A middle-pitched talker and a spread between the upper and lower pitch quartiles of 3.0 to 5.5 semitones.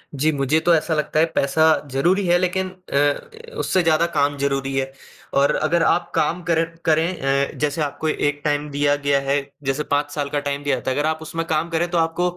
No: medium, 150 Hz; narrow, 2.6 semitones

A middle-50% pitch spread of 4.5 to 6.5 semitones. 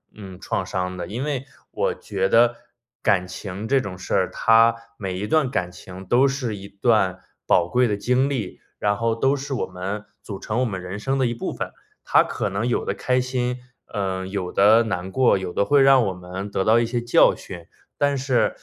Yes: average, 4.8 semitones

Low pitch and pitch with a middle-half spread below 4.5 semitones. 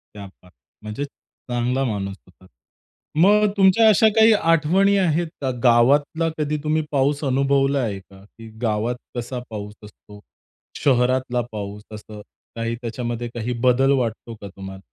No: low, 125 Hz; wide, 5.7 semitones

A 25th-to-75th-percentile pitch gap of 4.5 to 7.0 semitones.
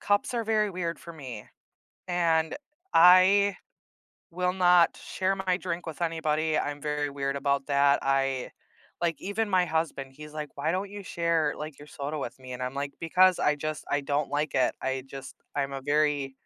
No: average, 4.1 semitones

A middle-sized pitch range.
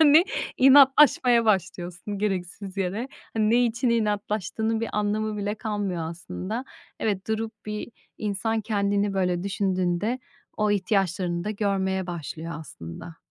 Yes: average, 3.0 semitones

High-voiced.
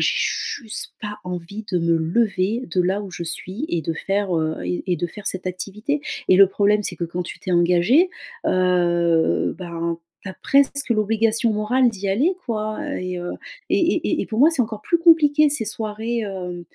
Yes: high, 200 Hz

